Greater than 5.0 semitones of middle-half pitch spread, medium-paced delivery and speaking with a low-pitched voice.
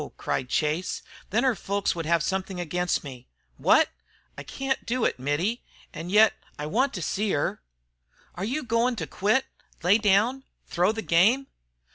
No: wide, 5.5 semitones; average, 170 wpm; high, 195 Hz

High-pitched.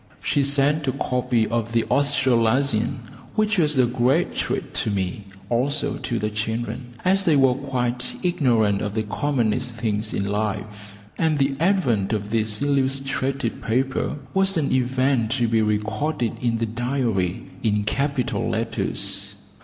No: low, 125 Hz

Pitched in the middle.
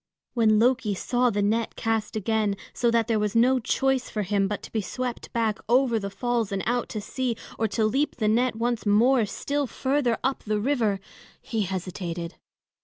No: high, 225 Hz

